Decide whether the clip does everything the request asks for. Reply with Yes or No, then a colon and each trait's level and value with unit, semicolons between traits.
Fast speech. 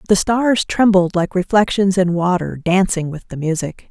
No: average, 170 wpm